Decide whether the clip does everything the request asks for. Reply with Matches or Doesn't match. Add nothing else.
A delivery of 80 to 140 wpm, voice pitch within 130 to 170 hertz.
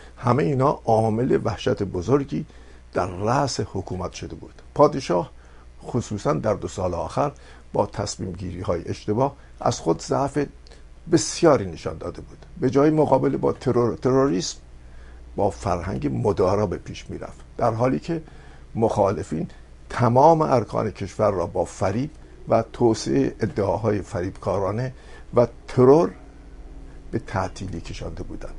Doesn't match